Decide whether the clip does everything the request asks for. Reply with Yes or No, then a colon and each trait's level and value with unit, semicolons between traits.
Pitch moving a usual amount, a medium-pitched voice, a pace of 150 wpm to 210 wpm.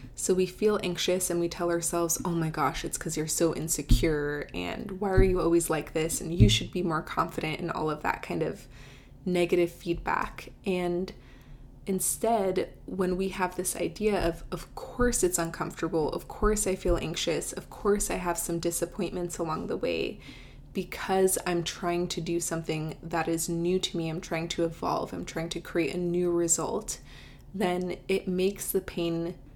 No: narrow, 2.0 semitones; medium, 170 Hz; average, 185 wpm